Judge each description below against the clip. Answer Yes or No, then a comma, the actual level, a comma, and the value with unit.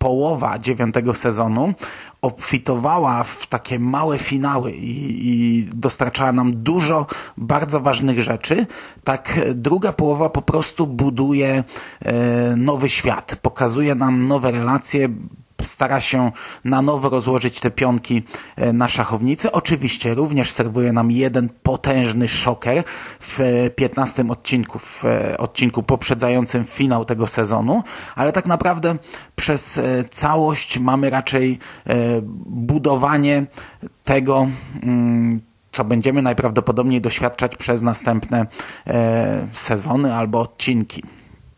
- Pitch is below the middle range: Yes, low, 125 Hz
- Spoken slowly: Yes, slow, 105 wpm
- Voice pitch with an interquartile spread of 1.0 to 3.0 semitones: Yes, average, 2.7 semitones